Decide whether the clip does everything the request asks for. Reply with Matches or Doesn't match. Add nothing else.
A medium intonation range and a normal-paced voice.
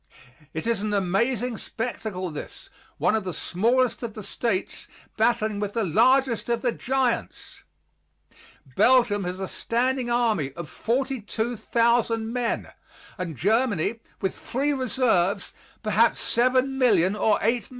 Doesn't match